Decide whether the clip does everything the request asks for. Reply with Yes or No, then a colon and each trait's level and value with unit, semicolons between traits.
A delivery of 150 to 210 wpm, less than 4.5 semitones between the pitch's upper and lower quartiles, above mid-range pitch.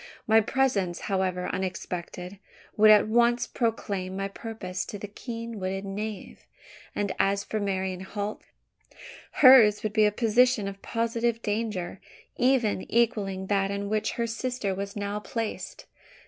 No: average, 140 wpm; average, 2.9 semitones; high, 210 Hz